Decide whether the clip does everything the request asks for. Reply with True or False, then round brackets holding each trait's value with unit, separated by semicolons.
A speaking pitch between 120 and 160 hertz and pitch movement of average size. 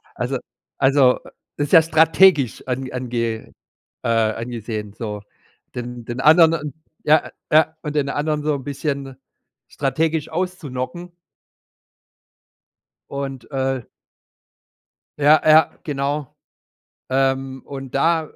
True (140 Hz; 3.5 semitones)